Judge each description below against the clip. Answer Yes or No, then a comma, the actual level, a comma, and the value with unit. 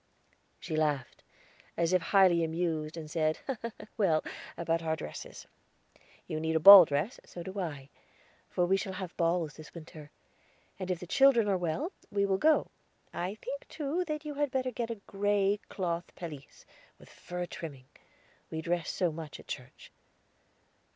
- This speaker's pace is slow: No, average, 165 wpm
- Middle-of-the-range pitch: Yes, medium, 175 Hz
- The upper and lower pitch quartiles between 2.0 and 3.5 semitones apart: No, average, 4.1 semitones